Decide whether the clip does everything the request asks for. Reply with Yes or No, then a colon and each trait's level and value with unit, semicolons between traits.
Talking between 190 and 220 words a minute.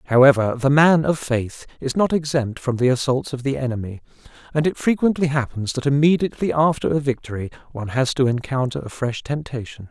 No: average, 180 wpm